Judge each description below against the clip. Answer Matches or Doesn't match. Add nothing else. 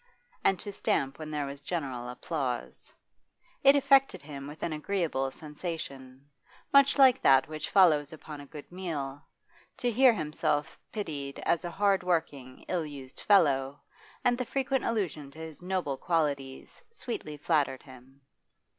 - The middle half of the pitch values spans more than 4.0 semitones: Matches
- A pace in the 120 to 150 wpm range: Matches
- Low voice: Doesn't match